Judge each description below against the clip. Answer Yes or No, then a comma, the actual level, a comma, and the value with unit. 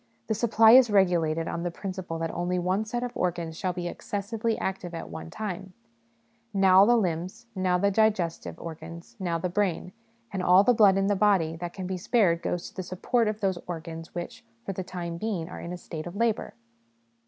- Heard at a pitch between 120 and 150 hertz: No, medium, 185 Hz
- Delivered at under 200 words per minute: No, fast, 205 wpm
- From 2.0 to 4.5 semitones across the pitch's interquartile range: Yes, average, 3.2 semitones